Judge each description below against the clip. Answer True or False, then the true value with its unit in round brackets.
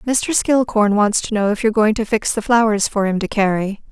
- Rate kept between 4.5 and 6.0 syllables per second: True (5.2 syllables/s)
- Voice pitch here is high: True (215 Hz)